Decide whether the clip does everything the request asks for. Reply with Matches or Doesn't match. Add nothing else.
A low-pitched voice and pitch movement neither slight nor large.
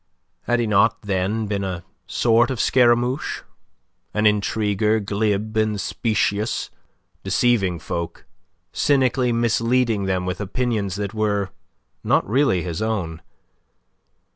Matches